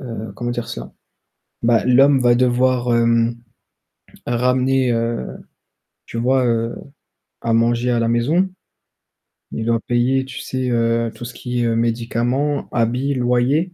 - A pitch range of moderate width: No, narrow, 1.6 semitones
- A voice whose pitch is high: No, low, 120 Hz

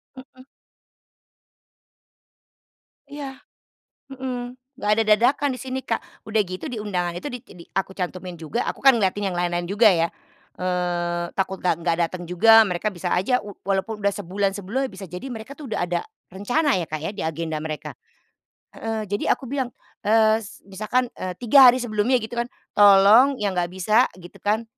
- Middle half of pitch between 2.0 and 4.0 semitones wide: No, average, 5.2 semitones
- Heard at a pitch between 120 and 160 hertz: No, high, 205 Hz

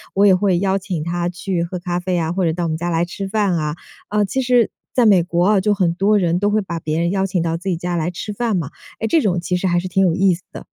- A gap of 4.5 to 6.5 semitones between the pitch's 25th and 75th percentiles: No, narrow, 2.5 semitones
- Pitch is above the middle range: No, medium, 180 Hz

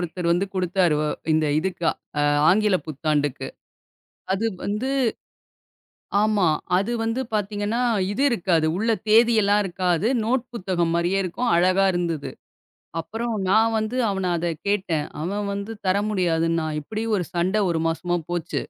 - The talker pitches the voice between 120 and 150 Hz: No, medium, 185 Hz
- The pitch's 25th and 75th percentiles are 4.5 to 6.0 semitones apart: No, average, 3.8 semitones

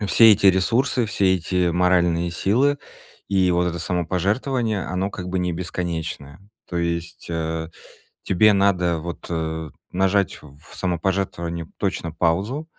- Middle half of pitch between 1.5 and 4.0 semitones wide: Yes, average, 2.7 semitones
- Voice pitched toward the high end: No, very low, 90 Hz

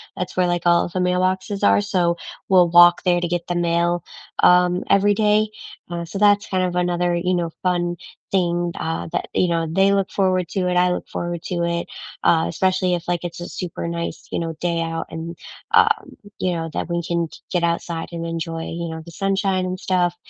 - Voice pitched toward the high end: No, medium, 175 Hz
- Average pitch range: No, narrow, 1.4 semitones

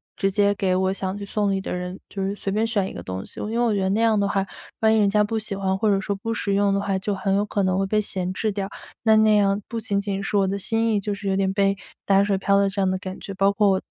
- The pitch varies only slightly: Yes, narrow, 1.4 semitones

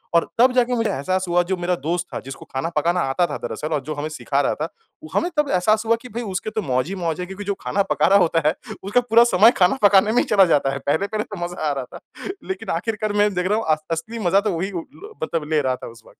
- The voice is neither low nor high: Yes, medium, 180 Hz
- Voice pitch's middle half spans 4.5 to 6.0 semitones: Yes, average, 5.1 semitones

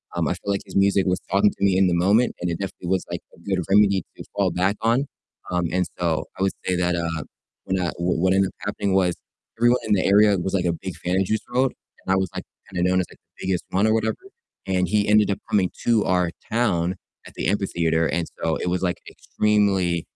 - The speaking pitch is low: Yes, very low, 95 Hz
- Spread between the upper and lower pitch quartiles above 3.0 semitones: No, narrow, 2.5 semitones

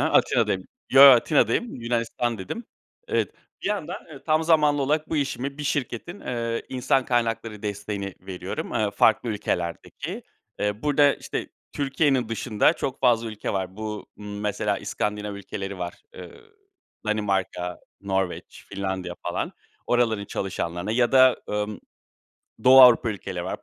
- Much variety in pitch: No, average, 5.0 semitones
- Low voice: Yes, low, 115 Hz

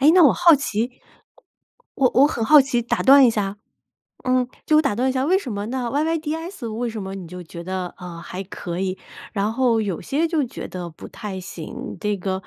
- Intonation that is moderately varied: No, wide, 6.5 semitones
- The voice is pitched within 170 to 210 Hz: No, high, 230 Hz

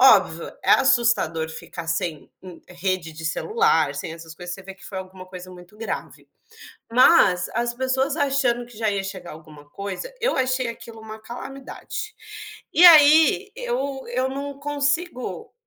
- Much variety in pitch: Yes, wide, 7.5 semitones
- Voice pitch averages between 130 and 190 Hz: No, high, 220 Hz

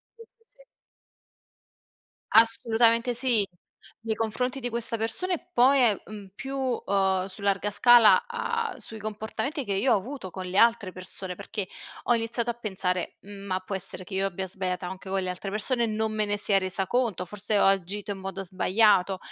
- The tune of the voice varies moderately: Yes, average, 3.5 semitones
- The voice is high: Yes, high, 210 Hz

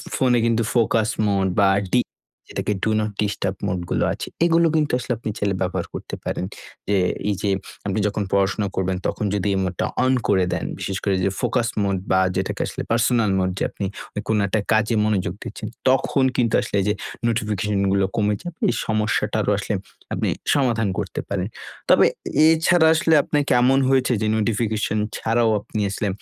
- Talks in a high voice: No, low, 110 Hz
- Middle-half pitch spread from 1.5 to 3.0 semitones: No, average, 3.4 semitones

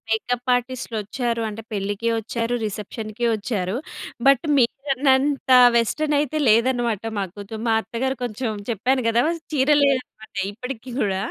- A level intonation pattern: No, average, 3.5 semitones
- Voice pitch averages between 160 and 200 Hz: No, high, 235 Hz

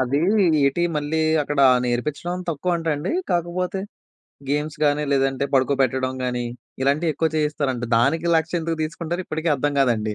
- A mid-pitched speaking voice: Yes, medium, 145 Hz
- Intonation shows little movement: No, average, 3.5 semitones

